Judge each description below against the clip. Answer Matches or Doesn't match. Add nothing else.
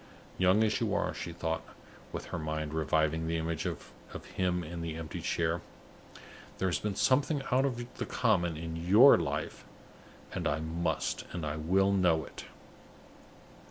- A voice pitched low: Matches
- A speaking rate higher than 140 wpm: Matches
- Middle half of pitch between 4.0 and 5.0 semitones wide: Doesn't match